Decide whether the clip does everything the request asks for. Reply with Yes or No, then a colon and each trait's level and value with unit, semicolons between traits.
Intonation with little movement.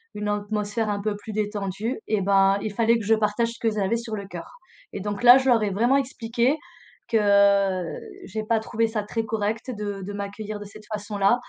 Yes: narrow, 1.9 semitones